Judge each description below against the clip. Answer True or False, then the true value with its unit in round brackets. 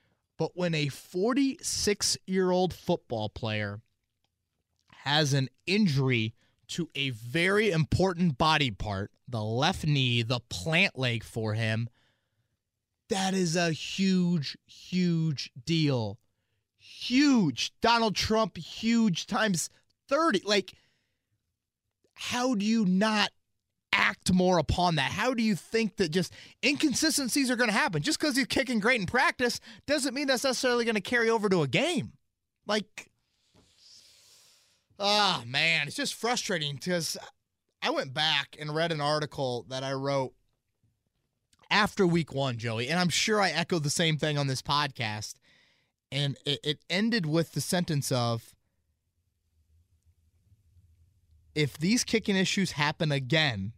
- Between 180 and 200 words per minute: False (135 wpm)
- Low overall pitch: False (150 Hz)